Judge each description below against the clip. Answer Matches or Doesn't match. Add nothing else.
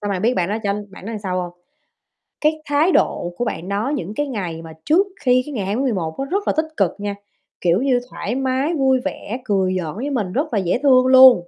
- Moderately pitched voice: Doesn't match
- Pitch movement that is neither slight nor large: Doesn't match